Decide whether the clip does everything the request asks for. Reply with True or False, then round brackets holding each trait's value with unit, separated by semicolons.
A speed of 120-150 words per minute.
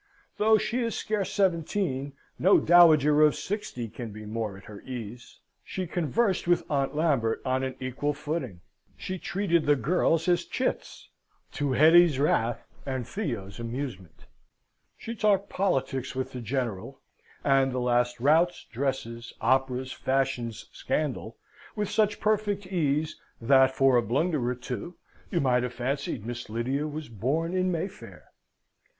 True (145 wpm)